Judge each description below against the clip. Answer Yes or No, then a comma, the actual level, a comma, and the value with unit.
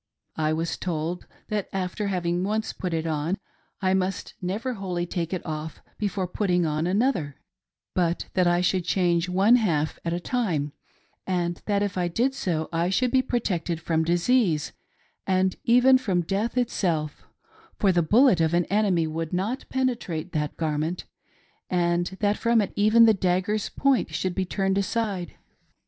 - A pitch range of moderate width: Yes, average, 3.7 semitones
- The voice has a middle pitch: Yes, medium, 180 Hz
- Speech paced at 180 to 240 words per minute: No, average, 165 wpm